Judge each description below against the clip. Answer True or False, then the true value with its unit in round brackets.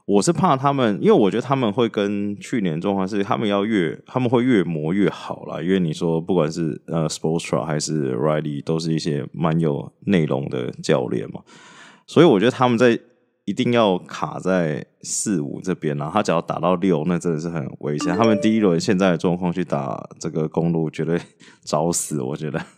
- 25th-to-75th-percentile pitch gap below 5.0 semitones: True (4.4 semitones)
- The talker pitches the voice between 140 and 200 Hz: False (90 Hz)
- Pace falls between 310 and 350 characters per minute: True (320 characters per minute)